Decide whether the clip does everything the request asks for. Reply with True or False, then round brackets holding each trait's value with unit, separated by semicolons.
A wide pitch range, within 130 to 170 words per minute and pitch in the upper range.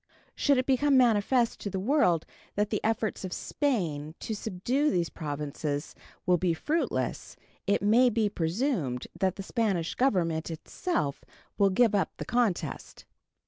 True (6.6 semitones; 145 wpm; 205 Hz)